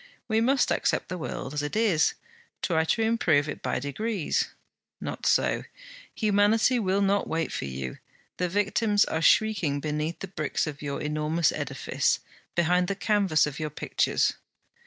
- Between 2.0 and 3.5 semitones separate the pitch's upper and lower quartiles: No, wide, 5.5 semitones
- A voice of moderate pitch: Yes, medium, 175 Hz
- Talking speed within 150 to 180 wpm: Yes, average, 155 wpm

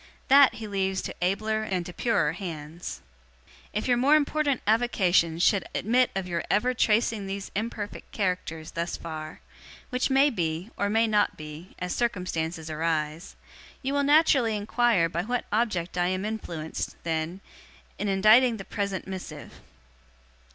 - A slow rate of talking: No, average, 150 wpm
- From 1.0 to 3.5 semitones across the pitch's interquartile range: No, average, 5.1 semitones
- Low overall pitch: No, high, 195 Hz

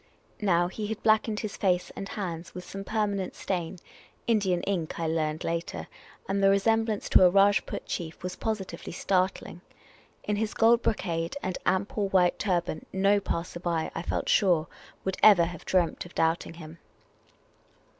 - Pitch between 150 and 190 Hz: Yes, medium, 185 Hz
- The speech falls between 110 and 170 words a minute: Yes, average, 165 wpm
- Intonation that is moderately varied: Yes, average, 3.1 semitones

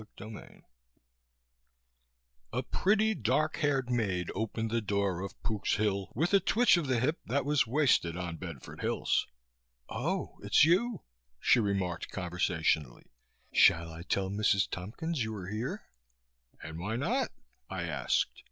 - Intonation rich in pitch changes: Yes, wide, 7.4 semitones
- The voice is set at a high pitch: No, low, 110 Hz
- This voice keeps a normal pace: Yes, average, 145 wpm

